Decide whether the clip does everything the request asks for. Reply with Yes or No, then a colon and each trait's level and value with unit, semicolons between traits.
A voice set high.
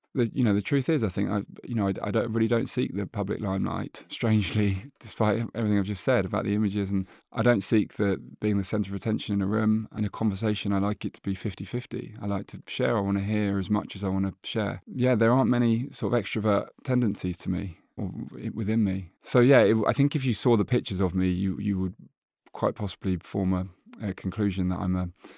No: low, 105 Hz